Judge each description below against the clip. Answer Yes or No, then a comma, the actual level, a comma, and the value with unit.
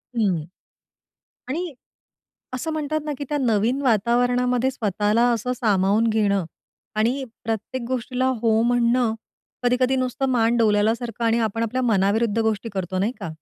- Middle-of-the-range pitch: No, high, 235 Hz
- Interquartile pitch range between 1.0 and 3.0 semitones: Yes, average, 2.7 semitones